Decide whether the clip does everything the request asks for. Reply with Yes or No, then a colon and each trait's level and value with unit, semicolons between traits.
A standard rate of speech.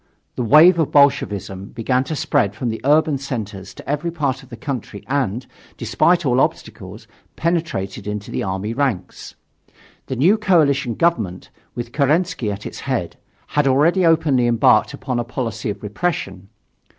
Yes: average, 155 wpm